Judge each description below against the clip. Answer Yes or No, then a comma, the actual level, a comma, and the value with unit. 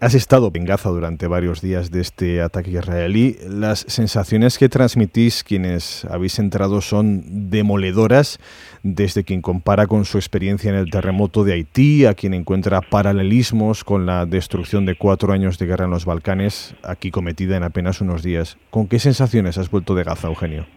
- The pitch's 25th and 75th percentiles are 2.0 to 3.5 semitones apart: Yes, average, 2.8 semitones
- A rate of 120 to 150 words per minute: No, average, 175 wpm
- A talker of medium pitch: No, very low, 95 Hz